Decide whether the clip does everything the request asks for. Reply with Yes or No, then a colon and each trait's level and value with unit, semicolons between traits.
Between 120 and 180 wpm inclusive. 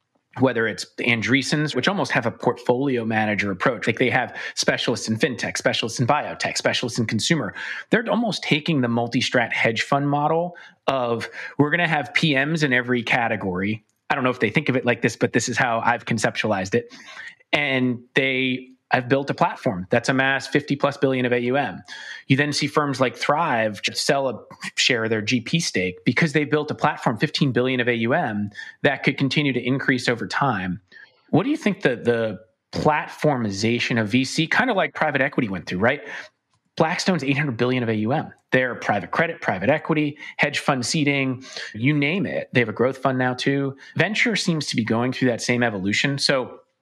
No: average, 190 wpm